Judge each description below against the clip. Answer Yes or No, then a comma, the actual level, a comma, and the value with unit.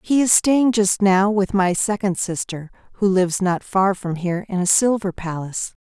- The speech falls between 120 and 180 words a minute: No, average, 195 wpm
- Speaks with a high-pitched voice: Yes, high, 195 Hz